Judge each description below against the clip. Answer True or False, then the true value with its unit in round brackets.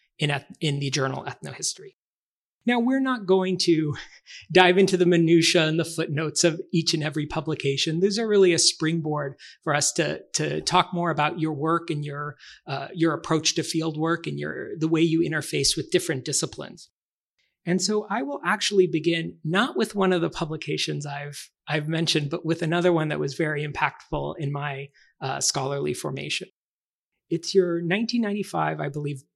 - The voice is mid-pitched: True (165 Hz)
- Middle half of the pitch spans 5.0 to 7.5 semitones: False (3.1 semitones)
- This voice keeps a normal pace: True (175 wpm)